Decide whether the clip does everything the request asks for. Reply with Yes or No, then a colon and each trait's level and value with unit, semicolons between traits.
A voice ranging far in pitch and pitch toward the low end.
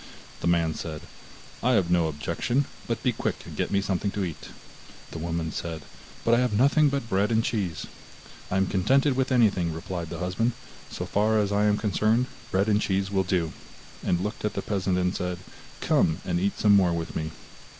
No: average, 4.2 semitones; very low, 95 Hz